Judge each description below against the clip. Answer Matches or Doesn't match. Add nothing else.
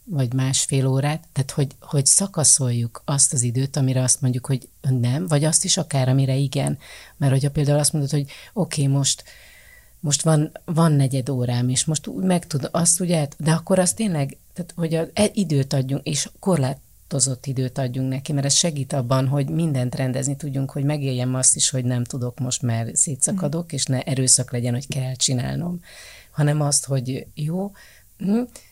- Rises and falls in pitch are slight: Doesn't match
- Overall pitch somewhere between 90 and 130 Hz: Doesn't match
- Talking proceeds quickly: Matches